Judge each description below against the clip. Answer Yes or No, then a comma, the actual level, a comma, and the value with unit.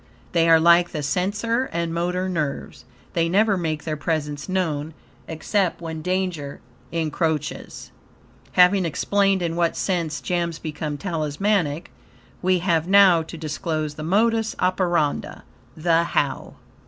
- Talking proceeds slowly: Yes, slow, 130 wpm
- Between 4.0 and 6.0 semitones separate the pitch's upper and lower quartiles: No, average, 2.9 semitones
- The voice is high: No, medium, 170 Hz